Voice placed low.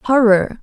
No: high, 225 Hz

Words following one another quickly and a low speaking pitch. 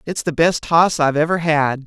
No: fast, 225 wpm; medium, 155 Hz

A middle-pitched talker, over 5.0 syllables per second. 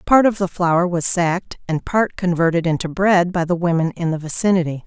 Yes: medium, 175 Hz; 5.4 syllables/s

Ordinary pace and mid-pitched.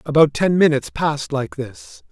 Yes: average, 170 wpm; medium, 145 Hz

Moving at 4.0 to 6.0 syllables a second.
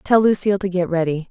No: 6.3 syllables/s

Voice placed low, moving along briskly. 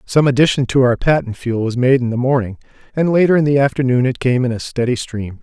Yes: low, 130 Hz; fast, 245 wpm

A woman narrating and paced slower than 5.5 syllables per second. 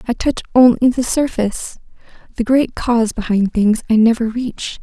Yes: female; 5.0 syllables/s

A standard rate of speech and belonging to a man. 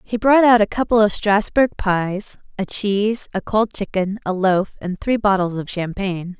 No: average, 190 wpm; female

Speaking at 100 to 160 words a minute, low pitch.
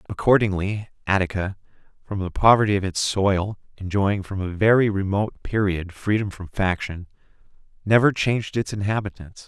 Yes: slow, 135 wpm; low, 100 Hz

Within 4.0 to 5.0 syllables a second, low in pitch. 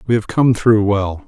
Yes: 4.5 syllables/s; low, 110 Hz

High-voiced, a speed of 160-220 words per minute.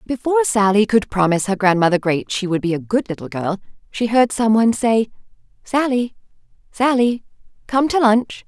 Yes: high, 220 Hz; average, 170 wpm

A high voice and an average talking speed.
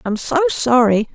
Yes: very high, 260 Hz; average, 155 wpm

